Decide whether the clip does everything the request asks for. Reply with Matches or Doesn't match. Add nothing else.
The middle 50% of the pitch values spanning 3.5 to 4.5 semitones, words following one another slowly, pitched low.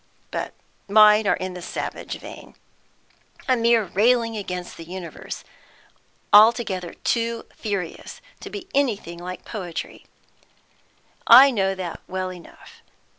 Doesn't match